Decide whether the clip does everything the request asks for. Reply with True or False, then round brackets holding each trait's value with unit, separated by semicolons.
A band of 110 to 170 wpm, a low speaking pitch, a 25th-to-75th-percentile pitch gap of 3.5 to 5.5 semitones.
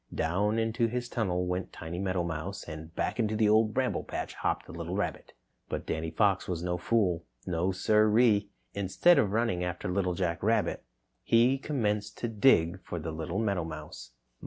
False (180 wpm; 95 Hz; 4.1 semitones)